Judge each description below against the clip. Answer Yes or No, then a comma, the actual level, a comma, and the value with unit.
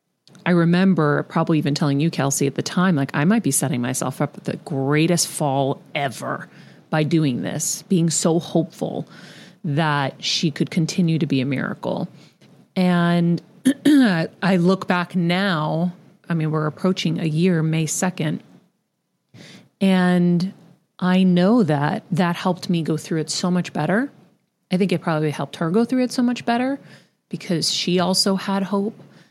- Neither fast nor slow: Yes, average, 160 wpm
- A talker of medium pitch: Yes, medium, 175 Hz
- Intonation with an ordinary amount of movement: Yes, average, 3.4 semitones